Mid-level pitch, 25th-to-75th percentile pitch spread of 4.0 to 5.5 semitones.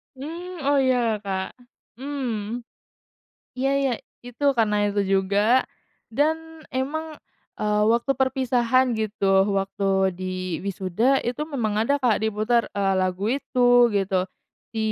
No: high, 230 Hz; average, 5.0 semitones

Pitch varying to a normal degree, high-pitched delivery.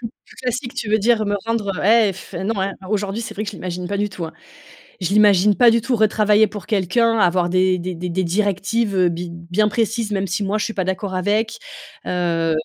Yes: average, 3.1 semitones; high, 205 Hz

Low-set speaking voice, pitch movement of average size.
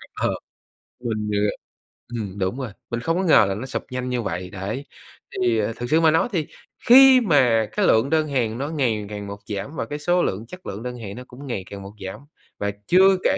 No: low, 120 Hz; wide, 6.7 semitones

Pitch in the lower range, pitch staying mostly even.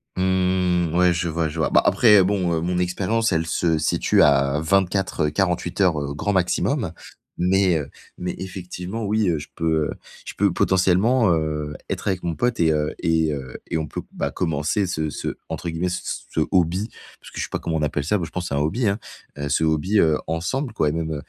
No: very low, 90 Hz; average, 3.2 semitones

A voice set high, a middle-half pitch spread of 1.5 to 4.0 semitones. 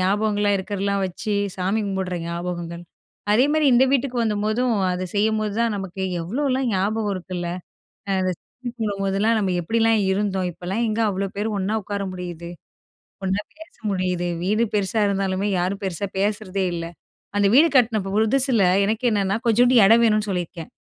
Yes: high, 200 Hz; average, 3.0 semitones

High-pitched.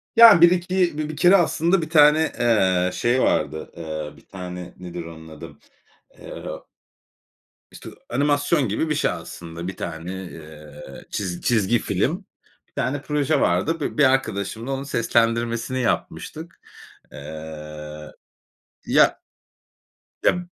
No: low, 115 Hz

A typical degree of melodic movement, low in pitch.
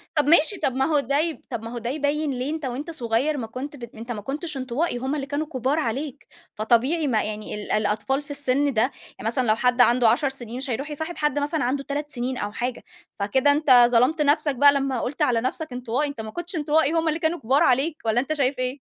No: average, 3.5 semitones; very high, 270 Hz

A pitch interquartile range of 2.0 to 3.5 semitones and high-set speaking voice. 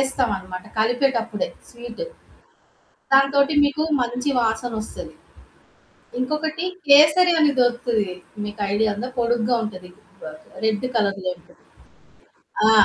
No: average, 4.2 semitones; high, 240 Hz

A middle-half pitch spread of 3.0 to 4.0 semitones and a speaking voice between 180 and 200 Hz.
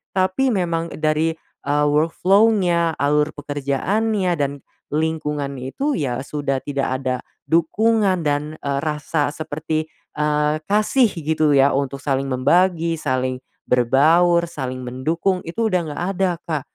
No: average, 3.7 semitones; medium, 155 Hz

